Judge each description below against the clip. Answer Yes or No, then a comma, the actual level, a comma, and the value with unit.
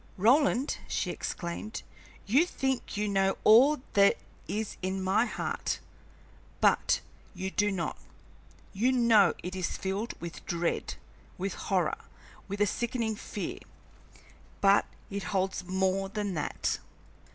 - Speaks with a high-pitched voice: Yes, high, 200 Hz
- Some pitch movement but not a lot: Yes, average, 3.2 semitones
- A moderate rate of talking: No, slow, 125 wpm